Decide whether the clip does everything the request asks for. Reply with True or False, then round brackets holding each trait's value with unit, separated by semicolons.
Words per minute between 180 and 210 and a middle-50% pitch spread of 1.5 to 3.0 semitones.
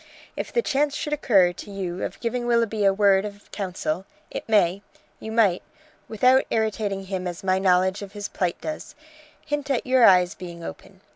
False (185 wpm; 3.9 semitones)